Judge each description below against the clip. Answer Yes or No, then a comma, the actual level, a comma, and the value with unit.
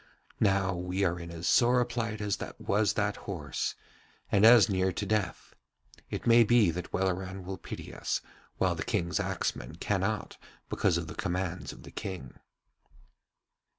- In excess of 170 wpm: No, average, 160 wpm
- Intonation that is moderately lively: Yes, average, 3.2 semitones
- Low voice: Yes, very low, 95 Hz